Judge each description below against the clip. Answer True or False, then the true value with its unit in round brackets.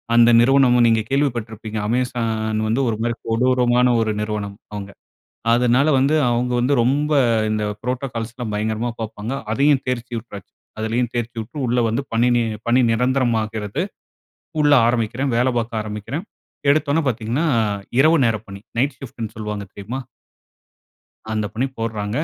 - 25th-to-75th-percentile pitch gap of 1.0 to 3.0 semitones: True (2.5 semitones)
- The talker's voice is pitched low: True (120 Hz)